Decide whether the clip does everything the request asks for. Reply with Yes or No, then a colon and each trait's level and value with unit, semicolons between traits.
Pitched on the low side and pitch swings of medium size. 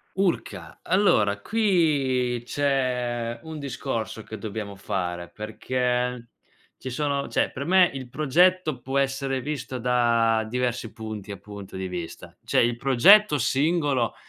Yes: low, 125 Hz; average, 3.9 semitones